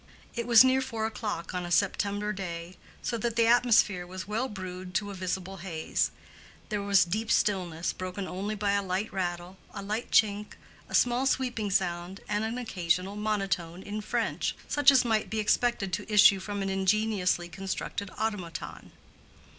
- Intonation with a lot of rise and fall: No, average, 2.9 semitones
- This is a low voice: No, high, 200 Hz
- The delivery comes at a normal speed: Yes, average, 170 wpm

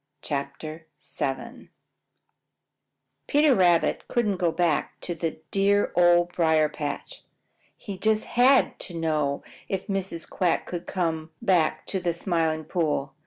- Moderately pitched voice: Yes, medium, 175 Hz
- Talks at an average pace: No, slow, 130 wpm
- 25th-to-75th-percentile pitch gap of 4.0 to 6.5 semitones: No, average, 3.6 semitones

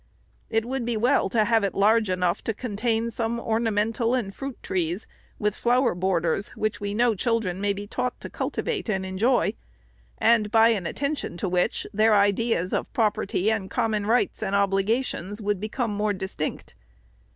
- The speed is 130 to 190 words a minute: Yes, average, 175 wpm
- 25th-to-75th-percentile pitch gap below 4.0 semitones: Yes, average, 3.0 semitones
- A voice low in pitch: No, high, 215 Hz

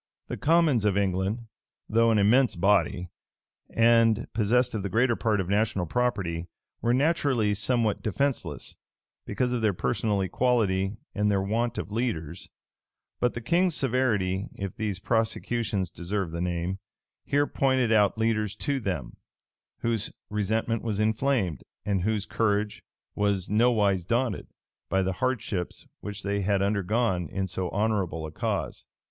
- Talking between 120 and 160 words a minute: Yes, average, 140 wpm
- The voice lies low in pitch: Yes, low, 105 Hz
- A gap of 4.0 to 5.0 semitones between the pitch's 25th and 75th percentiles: No, average, 3.4 semitones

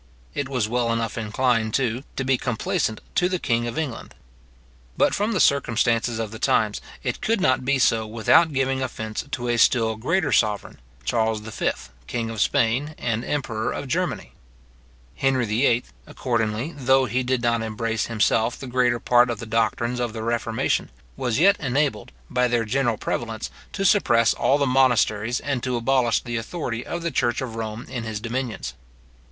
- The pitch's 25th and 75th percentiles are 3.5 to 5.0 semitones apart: No, average, 2.7 semitones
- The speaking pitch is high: No, low, 120 Hz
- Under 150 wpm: No, average, 175 wpm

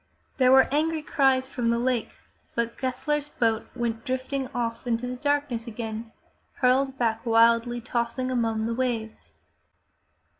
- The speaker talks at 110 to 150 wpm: Yes, average, 140 wpm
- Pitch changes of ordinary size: No, narrow, 2.2 semitones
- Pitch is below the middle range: No, high, 245 Hz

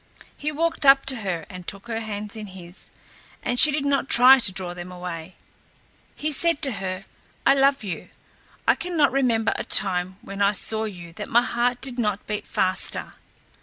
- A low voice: No, high, 220 Hz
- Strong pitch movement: Yes, wide, 6.3 semitones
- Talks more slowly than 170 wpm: No, average, 190 wpm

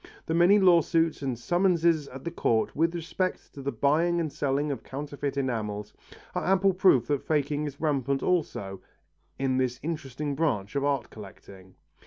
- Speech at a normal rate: Yes, average, 165 wpm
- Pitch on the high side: No, medium, 145 Hz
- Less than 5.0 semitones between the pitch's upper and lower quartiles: Yes, average, 4.1 semitones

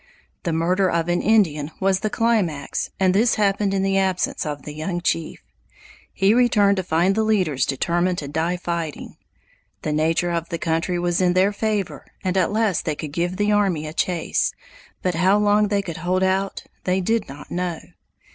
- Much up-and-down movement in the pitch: No, average, 3.2 semitones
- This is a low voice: No, medium, 180 Hz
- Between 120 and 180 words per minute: No, average, 190 wpm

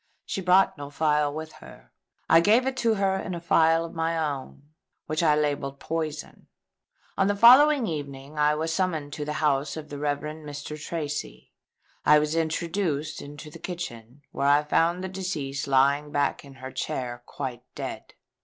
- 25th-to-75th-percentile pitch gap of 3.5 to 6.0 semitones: No, average, 2.7 semitones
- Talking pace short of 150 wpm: No, average, 175 wpm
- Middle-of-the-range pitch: Yes, medium, 150 Hz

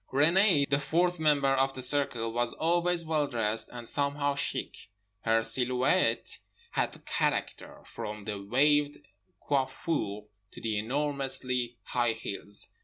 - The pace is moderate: No, slow, 125 wpm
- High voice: No, low, 135 Hz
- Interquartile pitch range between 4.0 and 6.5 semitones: Yes, average, 4.3 semitones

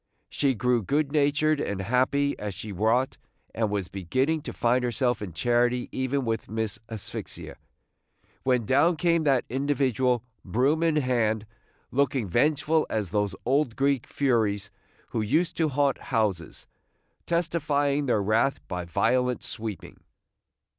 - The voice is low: Yes, low, 125 Hz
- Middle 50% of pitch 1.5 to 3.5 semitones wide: No, average, 4.6 semitones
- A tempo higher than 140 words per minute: No, slow, 135 wpm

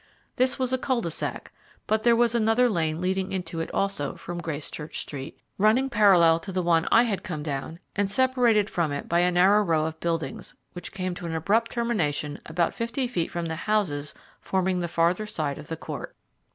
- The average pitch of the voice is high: No, medium, 180 Hz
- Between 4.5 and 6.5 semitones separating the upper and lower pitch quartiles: Yes, average, 4.8 semitones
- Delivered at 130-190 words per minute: No, fast, 205 wpm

